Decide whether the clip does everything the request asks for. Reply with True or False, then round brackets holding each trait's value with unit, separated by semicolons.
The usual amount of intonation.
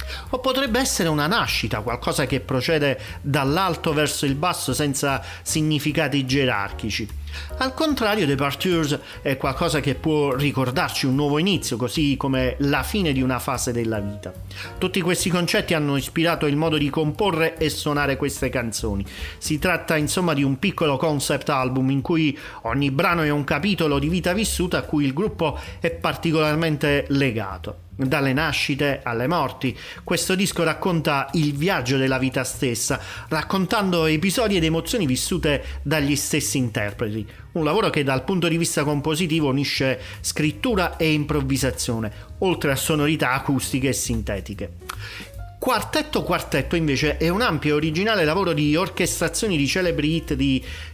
True (4.1 semitones)